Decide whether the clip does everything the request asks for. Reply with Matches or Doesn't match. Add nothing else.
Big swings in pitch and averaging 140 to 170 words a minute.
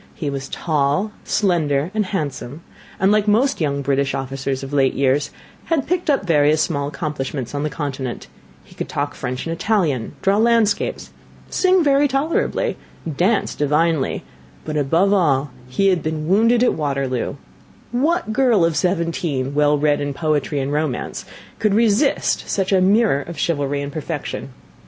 Matches